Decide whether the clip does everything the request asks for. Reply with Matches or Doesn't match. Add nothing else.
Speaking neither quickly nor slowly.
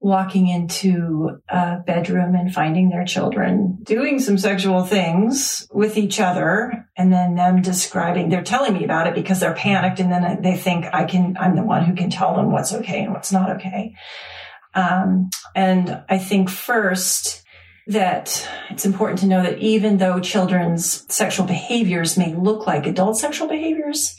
Matches